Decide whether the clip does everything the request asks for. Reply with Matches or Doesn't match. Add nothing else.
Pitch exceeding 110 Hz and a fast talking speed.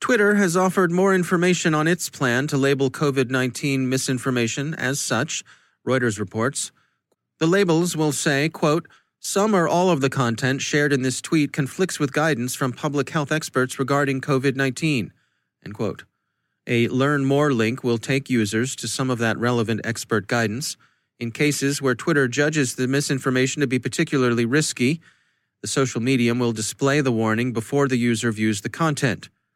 Doesn't match